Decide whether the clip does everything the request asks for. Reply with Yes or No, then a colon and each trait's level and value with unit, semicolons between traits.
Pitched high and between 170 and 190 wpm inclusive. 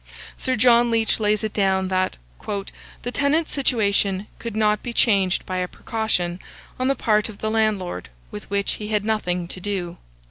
Yes: high, 210 Hz; average, 175 wpm